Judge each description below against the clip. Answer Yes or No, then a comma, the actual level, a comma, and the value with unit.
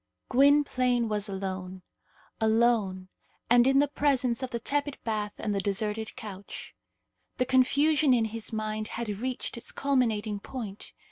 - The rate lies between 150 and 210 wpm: No, average, 140 wpm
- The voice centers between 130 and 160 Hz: No, high, 230 Hz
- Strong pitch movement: No, average, 3.8 semitones